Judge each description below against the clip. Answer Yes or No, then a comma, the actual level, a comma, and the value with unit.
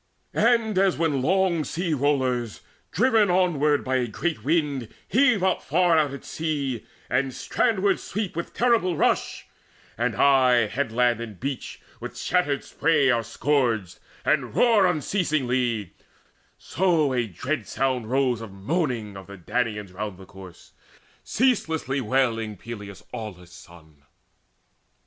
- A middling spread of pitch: No, wide, 6.6 semitones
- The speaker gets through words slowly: Yes, slow, 130 wpm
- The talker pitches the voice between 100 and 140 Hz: Yes, low, 135 Hz